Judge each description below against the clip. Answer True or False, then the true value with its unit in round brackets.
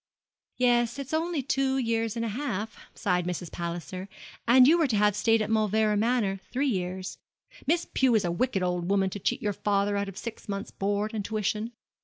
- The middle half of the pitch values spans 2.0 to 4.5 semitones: True (3.7 semitones)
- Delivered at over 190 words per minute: True (200 wpm)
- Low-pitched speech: False (215 Hz)